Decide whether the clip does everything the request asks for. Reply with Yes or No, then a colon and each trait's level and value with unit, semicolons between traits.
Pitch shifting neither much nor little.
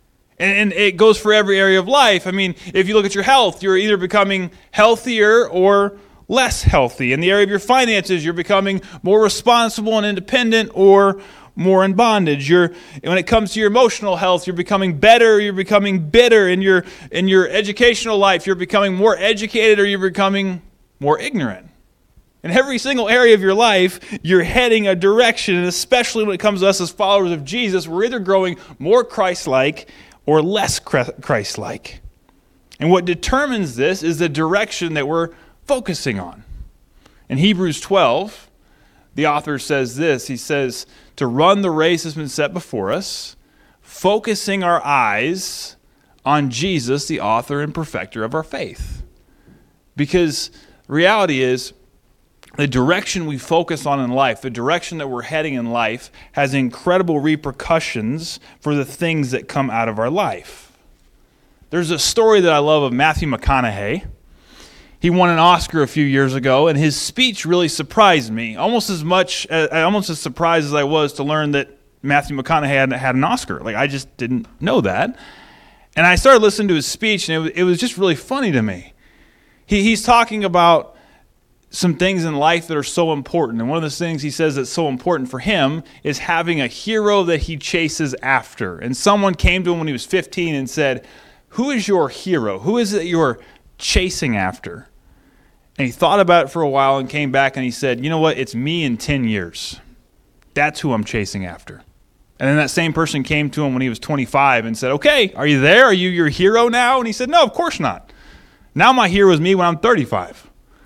No: wide, 5.7 semitones